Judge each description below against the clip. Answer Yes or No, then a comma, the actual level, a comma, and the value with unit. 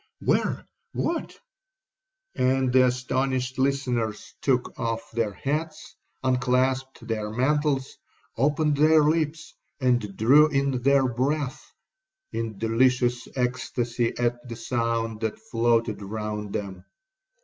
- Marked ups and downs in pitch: No, average, 3.1 semitones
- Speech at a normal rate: No, slow, 105 wpm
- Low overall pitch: Yes, low, 125 Hz